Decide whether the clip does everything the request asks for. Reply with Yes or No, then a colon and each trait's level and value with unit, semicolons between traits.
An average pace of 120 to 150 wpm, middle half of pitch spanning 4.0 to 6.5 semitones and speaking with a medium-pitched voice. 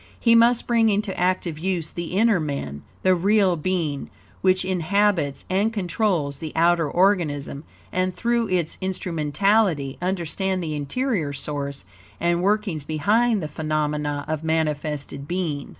Yes: slow, 135 wpm; average, 4.6 semitones; medium, 175 Hz